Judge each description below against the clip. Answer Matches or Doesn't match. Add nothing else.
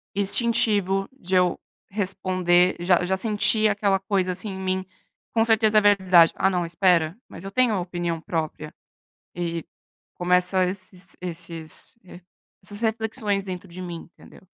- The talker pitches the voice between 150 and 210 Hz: Matches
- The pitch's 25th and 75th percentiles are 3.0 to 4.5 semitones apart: Doesn't match